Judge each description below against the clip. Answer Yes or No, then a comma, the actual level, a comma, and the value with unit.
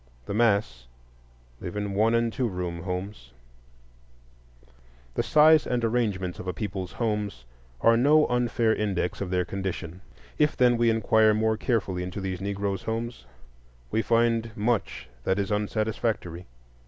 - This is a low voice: Yes, low, 105 Hz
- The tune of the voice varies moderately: Yes, average, 3.8 semitones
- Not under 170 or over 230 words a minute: No, average, 140 wpm